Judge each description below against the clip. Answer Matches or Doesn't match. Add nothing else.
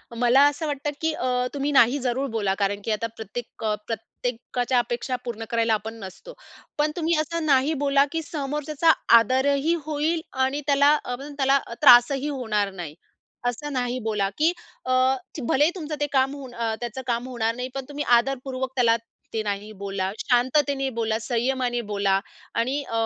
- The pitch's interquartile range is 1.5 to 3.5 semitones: Doesn't match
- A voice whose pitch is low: Doesn't match